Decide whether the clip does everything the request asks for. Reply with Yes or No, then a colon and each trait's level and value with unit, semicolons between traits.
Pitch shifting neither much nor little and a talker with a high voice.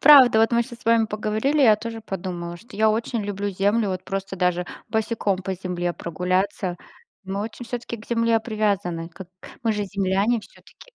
Yes: average, 3.3 semitones; high, 210 Hz